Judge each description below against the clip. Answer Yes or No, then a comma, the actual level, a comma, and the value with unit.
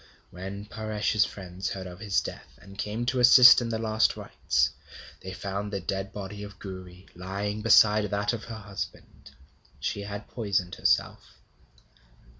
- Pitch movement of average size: No, narrow, 2.0 semitones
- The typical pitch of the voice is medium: No, low, 100 Hz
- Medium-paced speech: Yes, average, 155 wpm